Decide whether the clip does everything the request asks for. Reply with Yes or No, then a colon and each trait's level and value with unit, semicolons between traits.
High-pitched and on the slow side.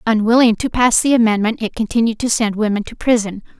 No: high, 225 Hz; average, 200 wpm